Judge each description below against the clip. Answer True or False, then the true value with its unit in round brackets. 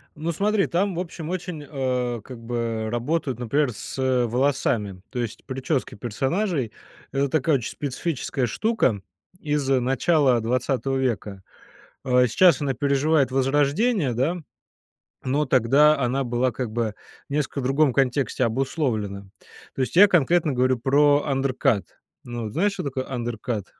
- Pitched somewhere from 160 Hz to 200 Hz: False (135 Hz)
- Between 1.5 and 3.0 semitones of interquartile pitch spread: False (3.7 semitones)